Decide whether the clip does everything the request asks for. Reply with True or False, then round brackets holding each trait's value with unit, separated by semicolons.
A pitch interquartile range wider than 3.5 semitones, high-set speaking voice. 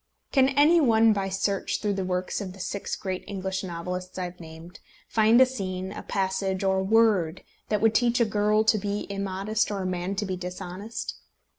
False (2.7 semitones; 195 Hz)